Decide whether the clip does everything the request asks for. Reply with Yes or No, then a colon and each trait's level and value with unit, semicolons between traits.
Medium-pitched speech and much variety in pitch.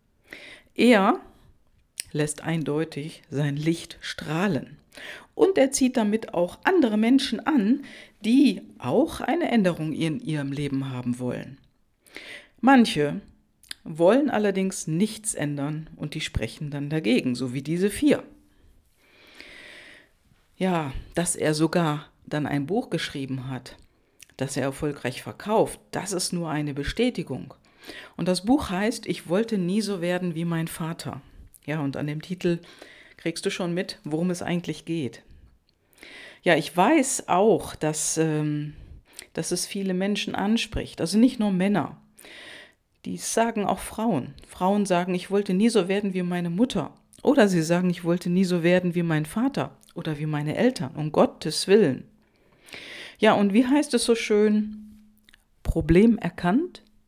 Yes: medium, 175 Hz; wide, 5.9 semitones